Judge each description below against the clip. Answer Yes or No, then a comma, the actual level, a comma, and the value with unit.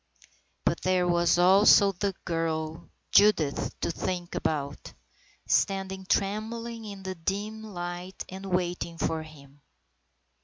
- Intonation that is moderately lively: Yes, average, 3.0 semitones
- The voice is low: No, medium, 185 Hz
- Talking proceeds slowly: Yes, slow, 115 wpm